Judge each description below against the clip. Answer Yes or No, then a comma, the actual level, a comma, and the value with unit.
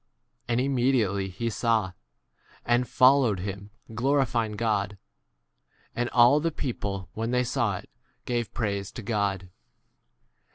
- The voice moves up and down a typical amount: Yes, average, 3.8 semitones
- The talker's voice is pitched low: Yes, low, 115 Hz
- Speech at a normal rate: No, slow, 130 wpm